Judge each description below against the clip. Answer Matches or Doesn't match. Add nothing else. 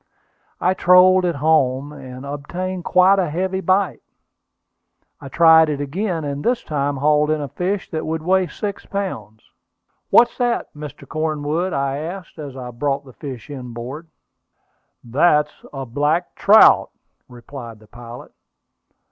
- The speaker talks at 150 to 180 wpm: Doesn't match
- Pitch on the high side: Doesn't match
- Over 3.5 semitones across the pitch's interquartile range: Matches